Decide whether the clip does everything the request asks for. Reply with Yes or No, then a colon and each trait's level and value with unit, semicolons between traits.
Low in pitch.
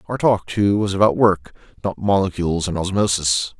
Yes: very low, 95 Hz